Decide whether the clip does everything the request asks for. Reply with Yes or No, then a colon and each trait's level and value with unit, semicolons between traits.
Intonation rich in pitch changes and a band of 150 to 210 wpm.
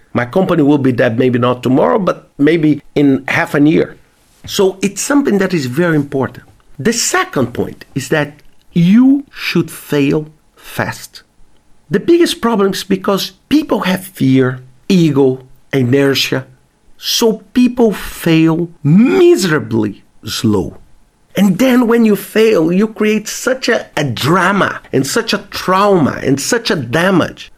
No: wide, 7.8 semitones; average, 140 wpm